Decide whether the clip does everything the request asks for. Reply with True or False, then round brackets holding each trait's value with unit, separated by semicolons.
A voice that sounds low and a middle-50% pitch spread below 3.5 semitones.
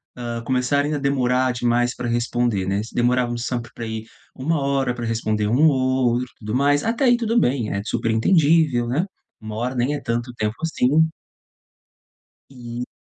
True (125 Hz; 2.9 semitones)